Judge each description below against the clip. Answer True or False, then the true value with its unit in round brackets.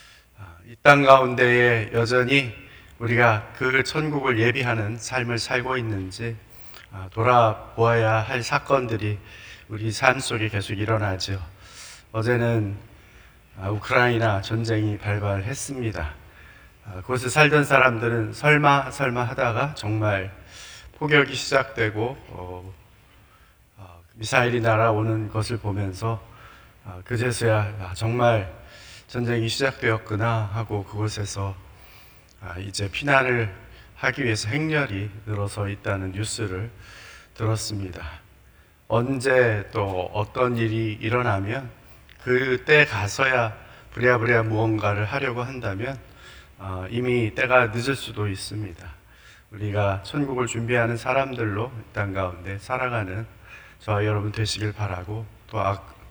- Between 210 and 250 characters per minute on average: True (245 characters per minute)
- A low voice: True (110 Hz)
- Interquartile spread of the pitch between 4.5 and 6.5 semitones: False (3.4 semitones)